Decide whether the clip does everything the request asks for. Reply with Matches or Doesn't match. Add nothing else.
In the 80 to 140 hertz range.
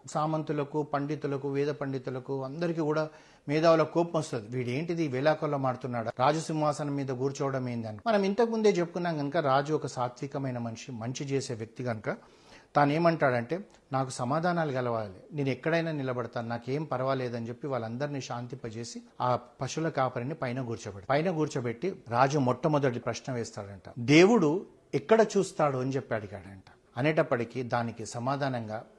Matches